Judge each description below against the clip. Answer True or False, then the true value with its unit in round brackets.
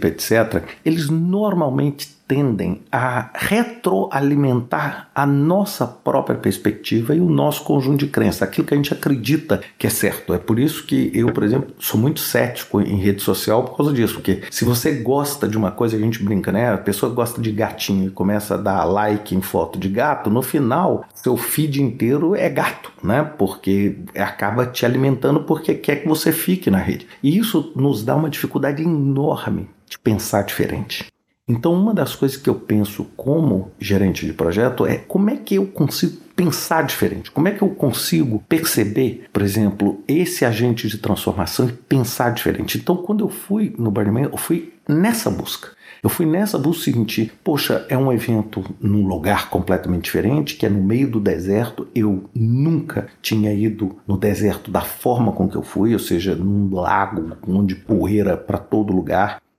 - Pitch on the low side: True (120 Hz)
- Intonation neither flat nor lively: False (6.7 semitones)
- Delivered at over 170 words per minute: True (180 wpm)